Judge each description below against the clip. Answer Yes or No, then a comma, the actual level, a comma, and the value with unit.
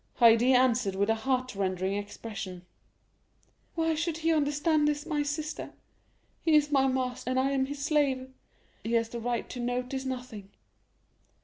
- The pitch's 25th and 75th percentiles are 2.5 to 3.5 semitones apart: No, average, 4.2 semitones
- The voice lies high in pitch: Yes, very high, 255 Hz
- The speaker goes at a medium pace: Yes, average, 150 wpm